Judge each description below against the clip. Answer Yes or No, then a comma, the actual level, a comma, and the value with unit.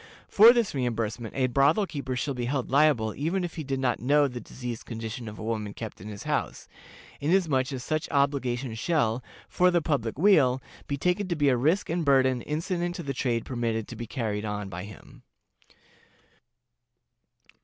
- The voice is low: Yes, low, 130 Hz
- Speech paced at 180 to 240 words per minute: Yes, average, 185 wpm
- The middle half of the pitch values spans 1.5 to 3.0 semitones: No, average, 4.9 semitones